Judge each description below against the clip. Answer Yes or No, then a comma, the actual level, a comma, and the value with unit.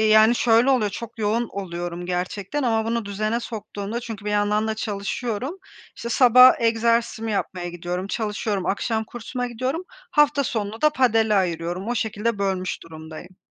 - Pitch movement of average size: Yes, average, 3.0 semitones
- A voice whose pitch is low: No, high, 220 Hz